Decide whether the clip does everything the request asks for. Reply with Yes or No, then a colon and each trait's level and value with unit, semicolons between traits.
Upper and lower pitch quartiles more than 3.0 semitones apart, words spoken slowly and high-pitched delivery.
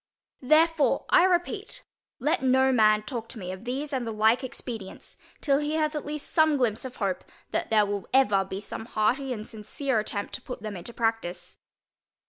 No: average, 5.1 semitones; average, 190 wpm; high, 245 Hz